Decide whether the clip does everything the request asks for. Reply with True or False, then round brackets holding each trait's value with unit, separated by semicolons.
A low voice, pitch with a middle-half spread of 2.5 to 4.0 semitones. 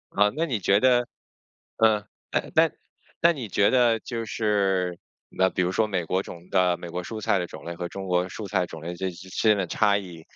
True (95 Hz; 3.5 semitones)